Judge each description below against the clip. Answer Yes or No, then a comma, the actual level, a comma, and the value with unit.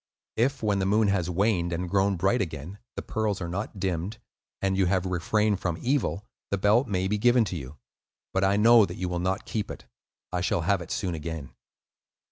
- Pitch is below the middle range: Yes, very low, 95 Hz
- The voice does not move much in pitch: No, average, 3.1 semitones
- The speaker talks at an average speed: No, fast, 210 wpm